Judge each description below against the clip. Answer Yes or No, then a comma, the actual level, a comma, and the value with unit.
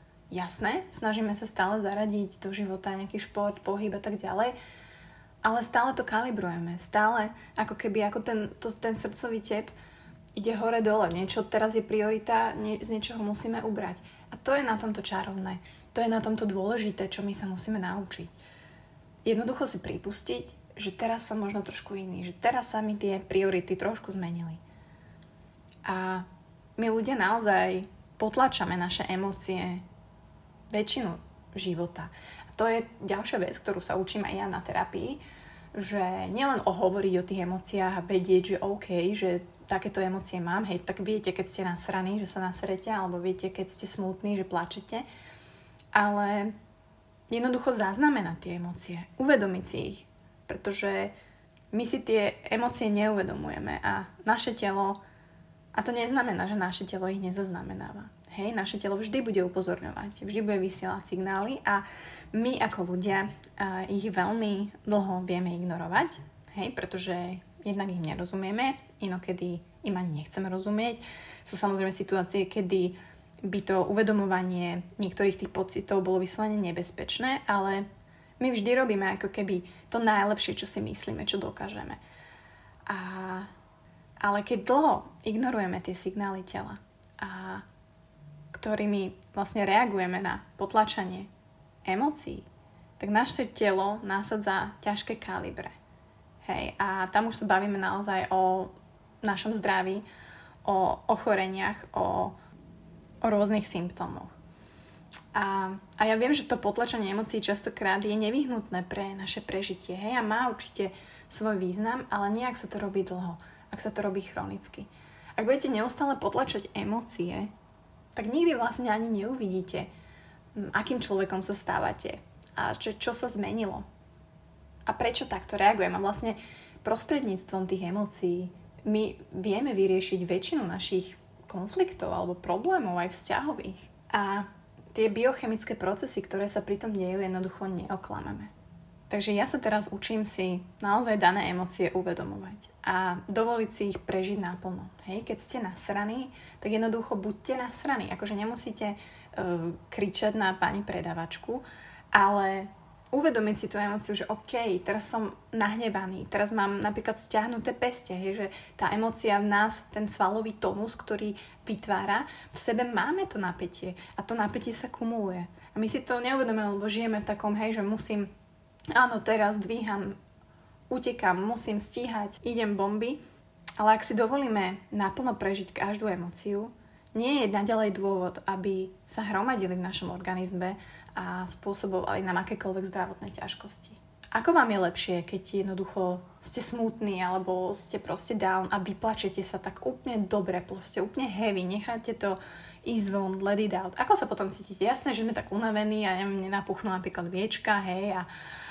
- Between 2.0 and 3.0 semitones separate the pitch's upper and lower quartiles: Yes, average, 2.7 semitones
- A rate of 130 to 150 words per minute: Yes, average, 145 wpm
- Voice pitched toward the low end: No, high, 200 Hz